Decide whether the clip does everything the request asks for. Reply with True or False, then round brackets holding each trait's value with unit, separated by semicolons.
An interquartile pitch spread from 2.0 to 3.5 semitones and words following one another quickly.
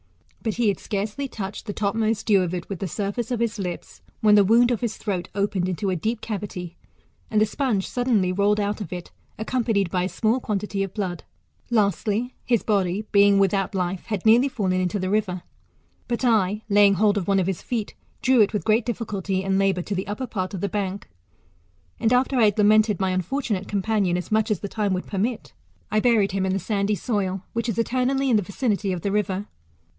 True (2.6 semitones; 215 wpm)